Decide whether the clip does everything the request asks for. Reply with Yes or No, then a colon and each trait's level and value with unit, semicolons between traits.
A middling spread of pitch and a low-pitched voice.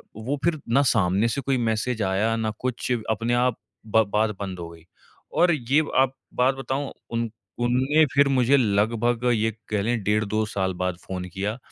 Yes: average, 3.4 semitones; low, 115 Hz